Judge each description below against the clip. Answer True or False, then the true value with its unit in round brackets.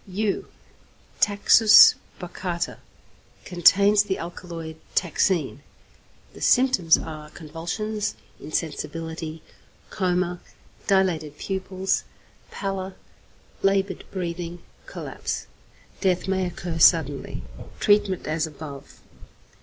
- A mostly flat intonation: False (3.0 semitones)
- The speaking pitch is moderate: True (180 Hz)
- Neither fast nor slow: False (80 wpm)